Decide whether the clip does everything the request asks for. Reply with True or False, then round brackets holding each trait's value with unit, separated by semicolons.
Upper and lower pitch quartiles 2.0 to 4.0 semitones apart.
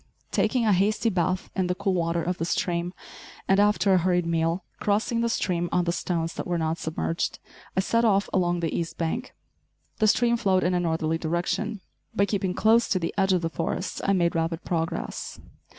True (3.1 semitones)